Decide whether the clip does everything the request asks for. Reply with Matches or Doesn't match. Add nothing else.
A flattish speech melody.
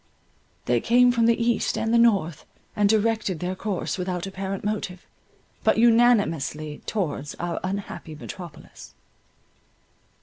Doesn't match